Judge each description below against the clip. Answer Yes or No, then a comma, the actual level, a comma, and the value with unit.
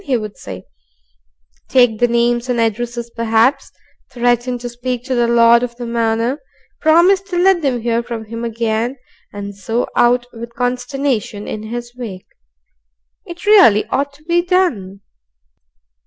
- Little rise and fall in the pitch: Yes, narrow, 2.1 semitones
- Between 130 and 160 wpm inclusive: Yes, average, 150 wpm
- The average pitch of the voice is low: No, high, 240 Hz